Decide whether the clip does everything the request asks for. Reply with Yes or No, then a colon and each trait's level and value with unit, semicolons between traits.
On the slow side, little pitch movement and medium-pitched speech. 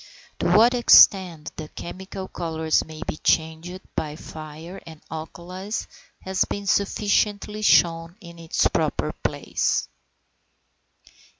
No: slow, 110 wpm; average, 3.3 semitones; medium, 170 Hz